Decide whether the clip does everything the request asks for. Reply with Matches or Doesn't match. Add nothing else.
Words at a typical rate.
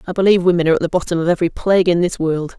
Doesn't match